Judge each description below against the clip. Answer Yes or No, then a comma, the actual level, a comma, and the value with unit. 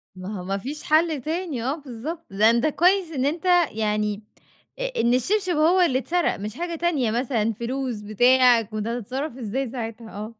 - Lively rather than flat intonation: Yes, wide, 6.1 semitones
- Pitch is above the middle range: Yes, very high, 255 Hz